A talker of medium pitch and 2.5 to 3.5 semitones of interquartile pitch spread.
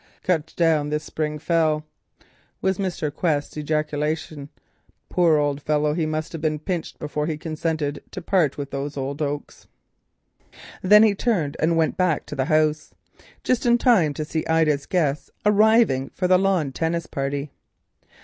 Yes: medium, 155 Hz; average, 2.8 semitones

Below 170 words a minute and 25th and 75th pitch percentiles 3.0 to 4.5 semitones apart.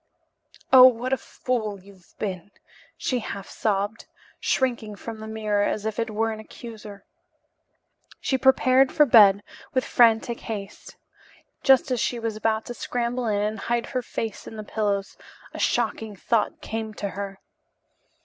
No: average, 155 wpm; narrow, 2.6 semitones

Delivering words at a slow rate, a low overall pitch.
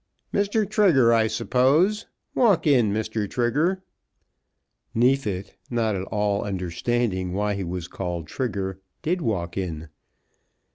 Yes: slow, 115 wpm; low, 110 Hz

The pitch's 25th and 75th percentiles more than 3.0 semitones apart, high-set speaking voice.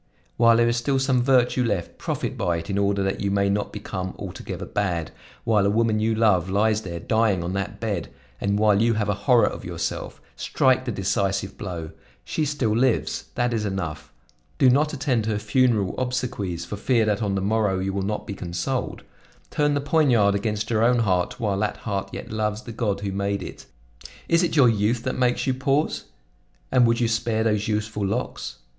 No: average, 3.4 semitones; low, 110 Hz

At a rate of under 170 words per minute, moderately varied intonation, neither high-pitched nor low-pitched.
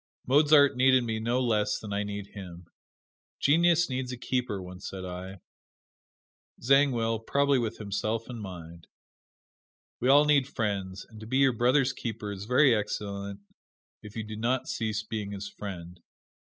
No: average, 155 wpm; average, 4.3 semitones; low, 110 Hz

